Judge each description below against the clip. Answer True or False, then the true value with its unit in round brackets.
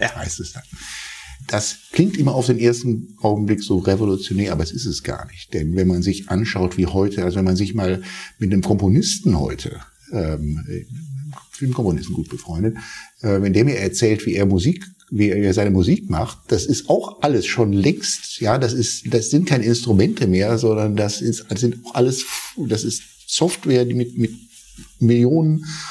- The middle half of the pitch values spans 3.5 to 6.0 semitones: True (4.2 semitones)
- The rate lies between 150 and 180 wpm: False (190 wpm)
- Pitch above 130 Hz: False (110 Hz)